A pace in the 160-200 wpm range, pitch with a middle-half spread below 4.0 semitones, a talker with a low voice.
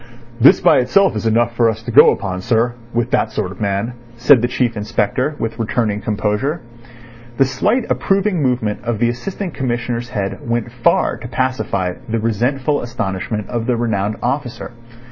Yes: average, 170 wpm; average, 2.9 semitones; low, 120 Hz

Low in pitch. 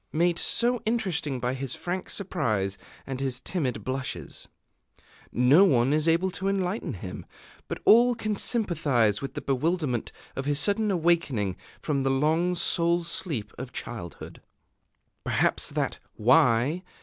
No: medium, 155 Hz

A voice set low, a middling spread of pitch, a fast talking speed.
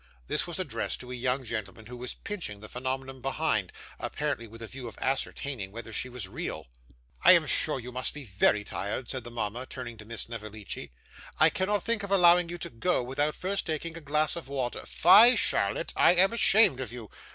No: low, 130 Hz; wide, 5.8 semitones; fast, 210 wpm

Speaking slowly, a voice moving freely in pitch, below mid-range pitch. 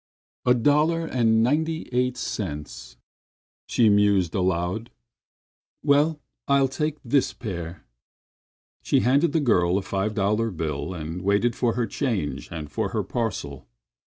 Yes: slow, 130 wpm; wide, 6.5 semitones; low, 110 Hz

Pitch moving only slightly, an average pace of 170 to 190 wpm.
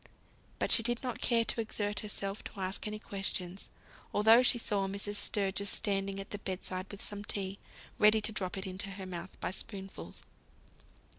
Yes: narrow, 1.7 semitones; average, 180 wpm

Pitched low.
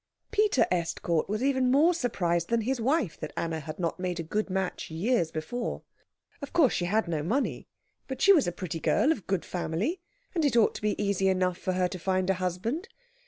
No: high, 195 Hz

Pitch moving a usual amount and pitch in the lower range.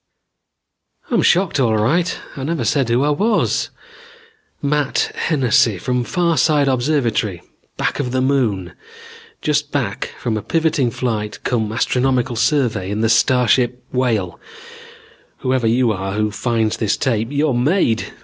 Yes: average, 4.4 semitones; low, 125 Hz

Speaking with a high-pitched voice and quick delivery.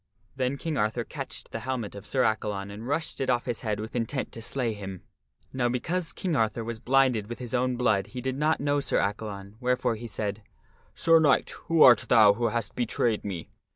No: low, 120 Hz; fast, 215 wpm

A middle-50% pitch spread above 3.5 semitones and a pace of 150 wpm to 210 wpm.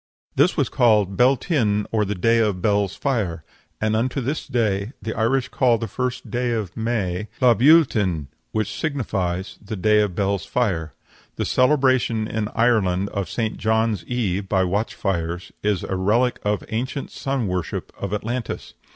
Yes: average, 3.9 semitones; average, 170 wpm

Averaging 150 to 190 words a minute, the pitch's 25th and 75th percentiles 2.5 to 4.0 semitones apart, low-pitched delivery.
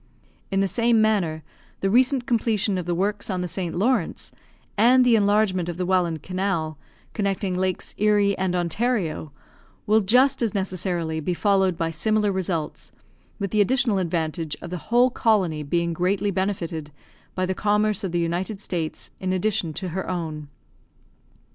No: average, 160 wpm; average, 3.6 semitones; high, 190 Hz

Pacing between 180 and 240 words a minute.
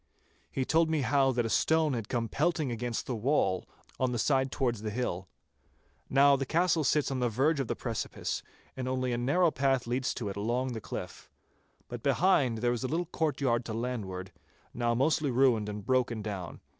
Yes: average, 195 wpm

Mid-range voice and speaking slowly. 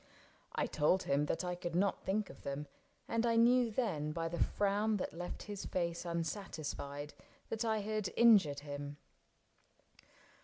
No: medium, 180 Hz; average, 155 wpm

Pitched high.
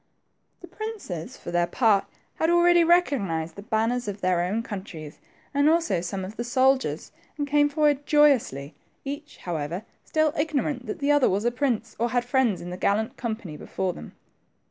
Yes: high, 240 Hz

